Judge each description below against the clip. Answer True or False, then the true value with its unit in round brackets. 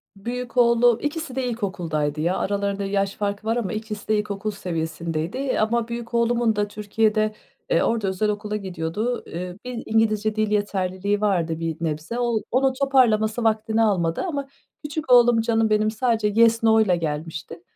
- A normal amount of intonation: True (3.5 semitones)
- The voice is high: True (215 Hz)